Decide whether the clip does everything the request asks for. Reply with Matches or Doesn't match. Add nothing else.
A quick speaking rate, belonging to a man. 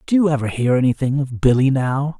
Matches